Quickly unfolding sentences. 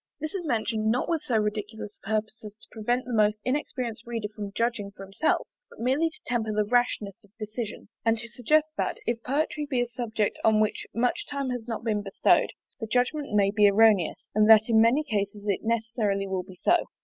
Yes: fast, 210 wpm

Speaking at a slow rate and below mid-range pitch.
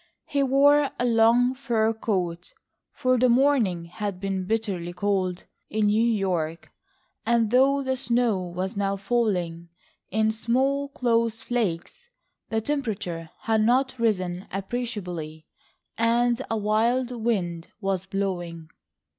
No: slow, 120 wpm; high, 220 Hz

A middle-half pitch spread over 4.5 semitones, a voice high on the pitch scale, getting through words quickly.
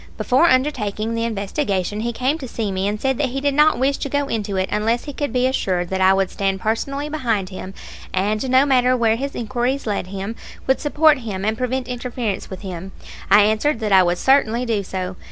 Yes: average, 5.0 semitones; high, 230 Hz; fast, 220 wpm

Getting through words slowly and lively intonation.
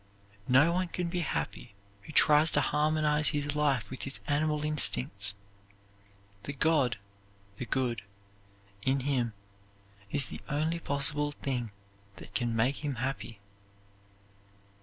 No: slow, 125 wpm; average, 3.2 semitones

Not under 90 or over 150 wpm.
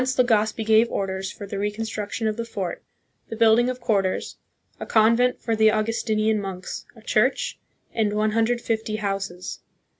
No: average, 160 wpm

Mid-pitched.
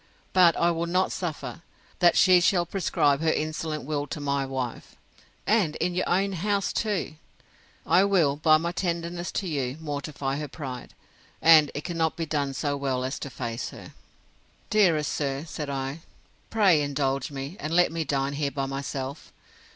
Yes: medium, 155 Hz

